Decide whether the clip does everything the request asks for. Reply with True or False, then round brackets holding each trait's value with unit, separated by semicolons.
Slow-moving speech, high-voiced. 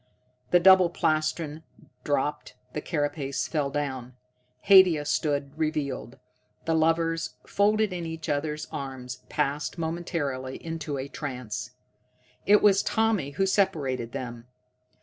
False (115 wpm; 150 Hz)